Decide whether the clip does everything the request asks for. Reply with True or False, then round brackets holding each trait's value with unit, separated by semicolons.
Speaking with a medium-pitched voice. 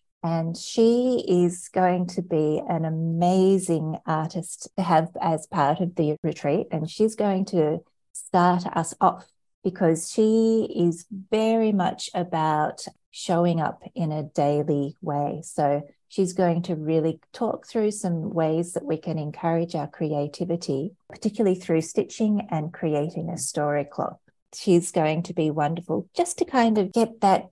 True (170 Hz)